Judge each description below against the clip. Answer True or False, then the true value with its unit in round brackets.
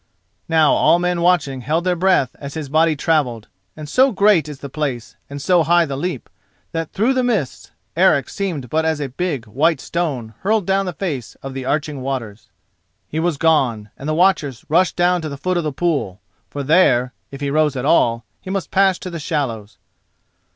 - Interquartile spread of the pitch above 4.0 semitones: True (4.6 semitones)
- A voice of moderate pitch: True (155 Hz)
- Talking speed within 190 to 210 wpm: True (200 wpm)